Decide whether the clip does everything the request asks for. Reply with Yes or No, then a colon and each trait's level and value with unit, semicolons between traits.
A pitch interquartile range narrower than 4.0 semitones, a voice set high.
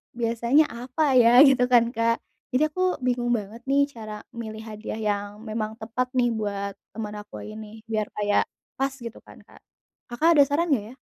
Yes: average, 2.8 semitones; high, 230 Hz